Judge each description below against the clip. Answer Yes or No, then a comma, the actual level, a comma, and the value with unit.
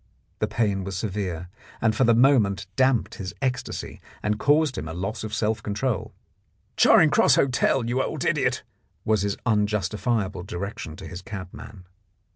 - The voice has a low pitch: Yes, low, 105 Hz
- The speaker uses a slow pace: No, average, 155 wpm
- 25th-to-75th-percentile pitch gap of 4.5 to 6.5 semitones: No, average, 3.5 semitones